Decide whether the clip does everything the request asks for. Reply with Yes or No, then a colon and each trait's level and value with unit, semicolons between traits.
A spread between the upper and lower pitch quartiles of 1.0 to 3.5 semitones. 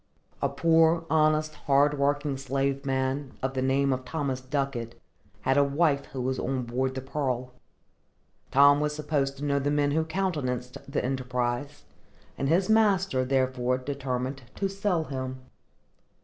Yes: narrow, 2.4 semitones